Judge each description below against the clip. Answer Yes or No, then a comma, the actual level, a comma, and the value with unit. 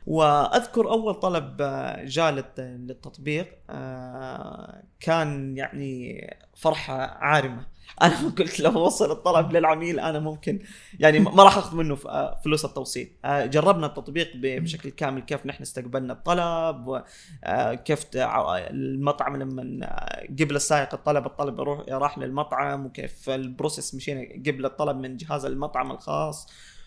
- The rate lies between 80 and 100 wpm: No, average, 115 wpm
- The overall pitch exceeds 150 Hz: No, medium, 145 Hz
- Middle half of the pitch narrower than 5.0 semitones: Yes, average, 3.5 semitones